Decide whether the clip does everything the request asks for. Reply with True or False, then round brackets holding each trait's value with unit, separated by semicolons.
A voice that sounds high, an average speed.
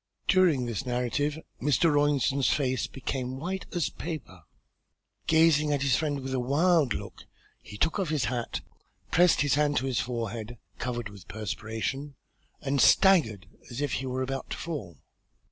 False (135 Hz; 160 wpm)